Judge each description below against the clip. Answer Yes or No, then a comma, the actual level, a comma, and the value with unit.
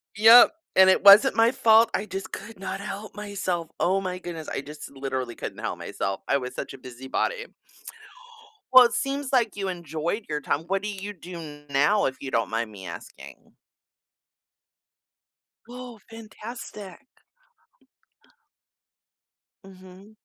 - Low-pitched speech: No, high, 190 Hz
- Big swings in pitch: Yes, wide, 6.4 semitones